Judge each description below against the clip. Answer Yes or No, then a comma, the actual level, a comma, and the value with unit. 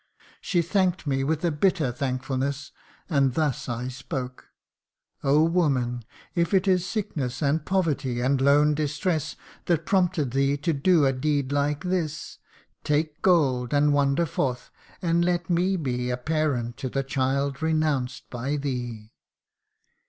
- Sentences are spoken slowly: No, average, 145 wpm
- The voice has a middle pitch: Yes, medium, 145 Hz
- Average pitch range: Yes, average, 3.9 semitones